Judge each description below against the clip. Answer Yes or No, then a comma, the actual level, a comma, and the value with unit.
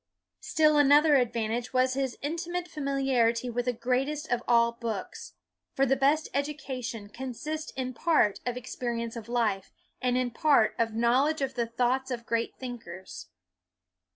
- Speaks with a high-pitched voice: Yes, very high, 250 Hz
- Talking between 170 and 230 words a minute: No, average, 155 wpm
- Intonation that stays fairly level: No, average, 3.0 semitones